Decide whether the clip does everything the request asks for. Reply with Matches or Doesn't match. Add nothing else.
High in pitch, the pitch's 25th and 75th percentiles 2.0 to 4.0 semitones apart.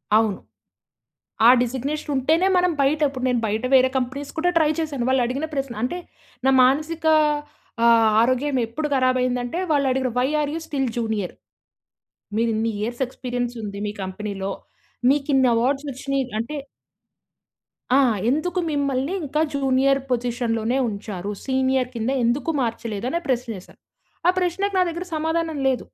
Matches